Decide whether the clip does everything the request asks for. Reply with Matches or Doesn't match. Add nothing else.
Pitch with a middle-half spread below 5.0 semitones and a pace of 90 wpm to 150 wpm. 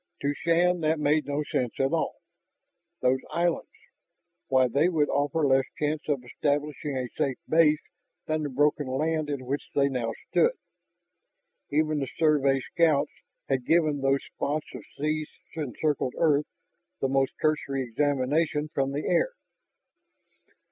Matches